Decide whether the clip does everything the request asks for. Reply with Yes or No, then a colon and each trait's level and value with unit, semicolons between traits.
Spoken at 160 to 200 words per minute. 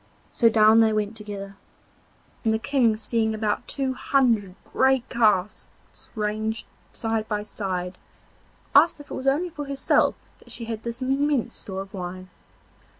No: average, 150 wpm